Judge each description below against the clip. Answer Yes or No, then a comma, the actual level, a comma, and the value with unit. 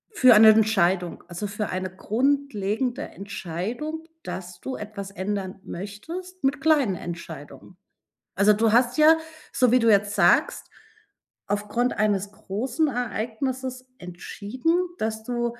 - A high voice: Yes, high, 215 Hz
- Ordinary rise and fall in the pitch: Yes, average, 4.5 semitones